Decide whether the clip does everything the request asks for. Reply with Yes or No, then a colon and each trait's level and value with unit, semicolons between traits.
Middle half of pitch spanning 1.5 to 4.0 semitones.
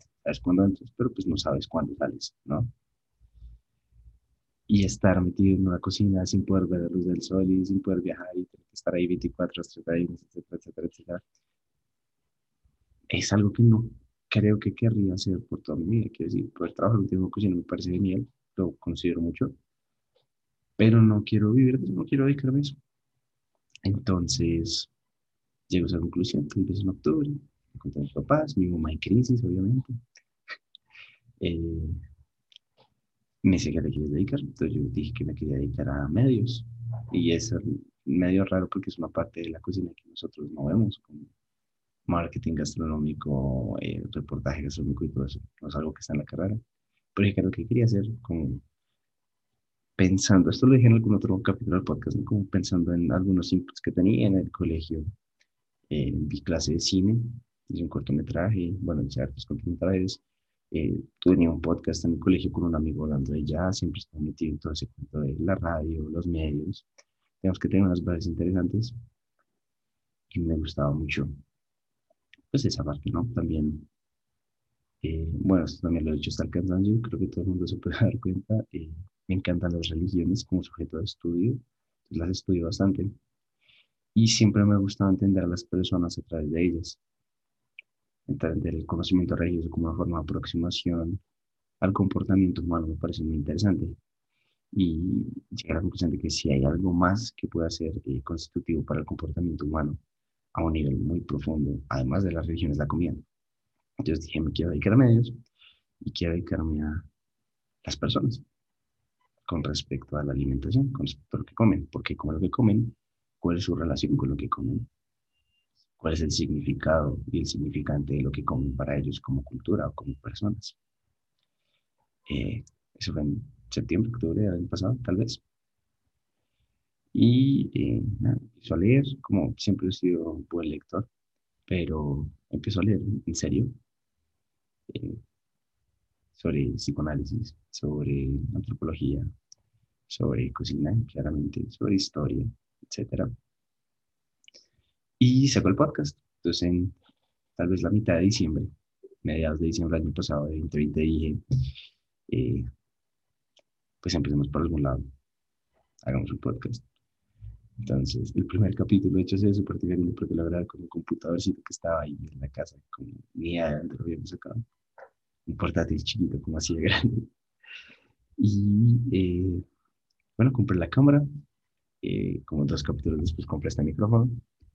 No: average, 4.6 semitones